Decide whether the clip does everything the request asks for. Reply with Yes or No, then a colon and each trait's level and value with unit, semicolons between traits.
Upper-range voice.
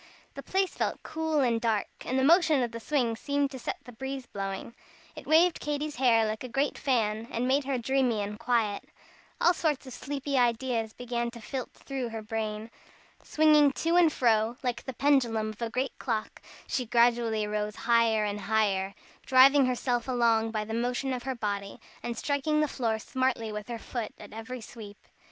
Yes: high, 240 Hz